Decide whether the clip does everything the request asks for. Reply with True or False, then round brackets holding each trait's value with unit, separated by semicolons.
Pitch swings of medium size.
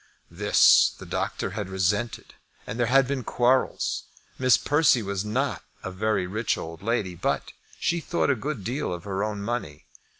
True (4.9 semitones)